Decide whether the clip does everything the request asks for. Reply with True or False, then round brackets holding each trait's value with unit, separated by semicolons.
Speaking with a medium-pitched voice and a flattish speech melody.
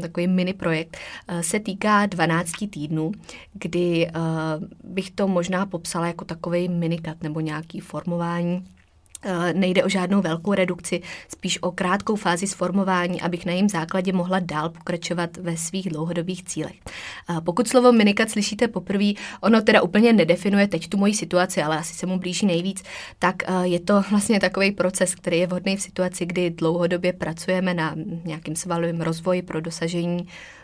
True (180 Hz; 2.2 semitones)